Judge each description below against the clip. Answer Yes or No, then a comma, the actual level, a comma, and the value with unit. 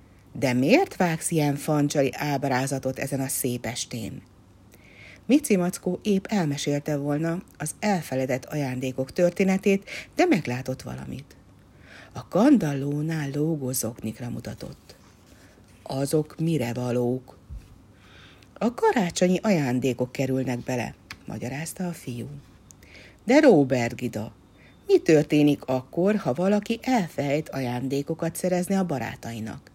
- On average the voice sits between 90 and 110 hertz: No, medium, 140 Hz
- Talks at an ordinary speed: No, slow, 100 wpm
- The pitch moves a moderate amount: No, wide, 6.5 semitones